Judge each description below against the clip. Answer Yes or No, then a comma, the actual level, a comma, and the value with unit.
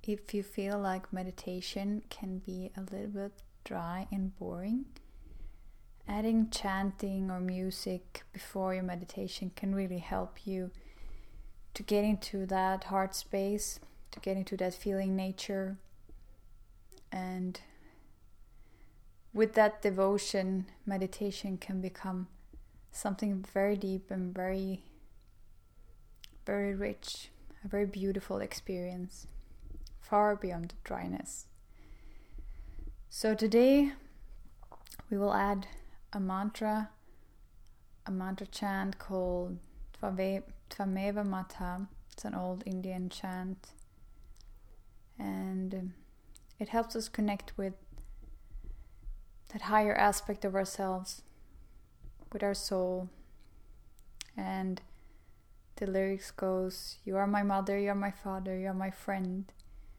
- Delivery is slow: Yes, slow, 105 wpm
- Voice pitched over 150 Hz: Yes, high, 190 Hz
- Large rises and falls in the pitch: Yes, wide, 7.0 semitones